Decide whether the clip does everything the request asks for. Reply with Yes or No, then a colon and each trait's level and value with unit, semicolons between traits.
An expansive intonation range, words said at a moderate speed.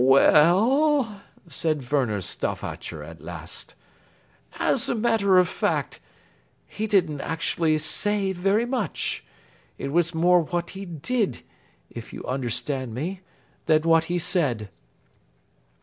No: wide, 5.8 semitones; slow, 125 wpm